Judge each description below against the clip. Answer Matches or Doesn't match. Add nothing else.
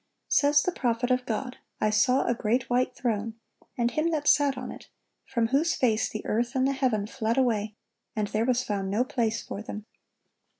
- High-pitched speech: Matches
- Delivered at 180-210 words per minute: Matches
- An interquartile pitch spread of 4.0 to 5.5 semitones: Doesn't match